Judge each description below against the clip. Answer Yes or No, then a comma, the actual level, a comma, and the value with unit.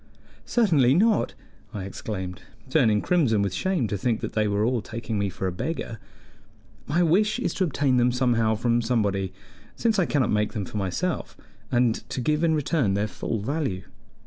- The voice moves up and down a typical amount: No, wide, 6.7 semitones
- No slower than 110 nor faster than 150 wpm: No, average, 180 wpm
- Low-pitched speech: Yes, low, 120 Hz